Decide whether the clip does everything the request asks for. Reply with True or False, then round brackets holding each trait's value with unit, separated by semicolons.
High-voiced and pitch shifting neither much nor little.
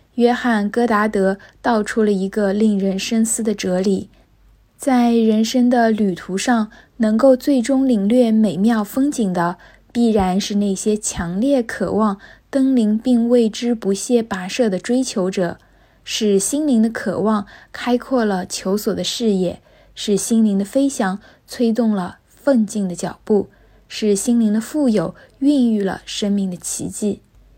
True (220 Hz; 3.6 semitones)